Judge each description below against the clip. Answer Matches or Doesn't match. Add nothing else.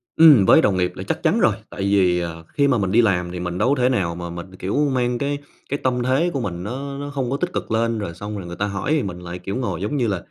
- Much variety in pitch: Matches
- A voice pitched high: Doesn't match